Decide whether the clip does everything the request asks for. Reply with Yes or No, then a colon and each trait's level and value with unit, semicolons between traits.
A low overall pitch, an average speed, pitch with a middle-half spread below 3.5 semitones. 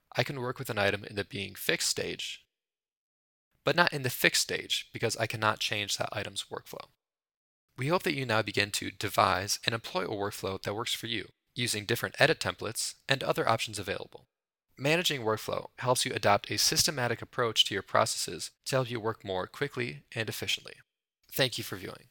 No: low, 115 Hz; average, 195 wpm; average, 3.9 semitones